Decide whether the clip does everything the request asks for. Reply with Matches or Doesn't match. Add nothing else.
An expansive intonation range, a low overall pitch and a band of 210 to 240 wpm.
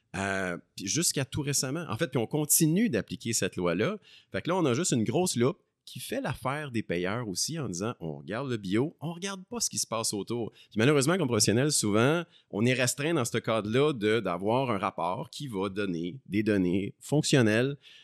Matches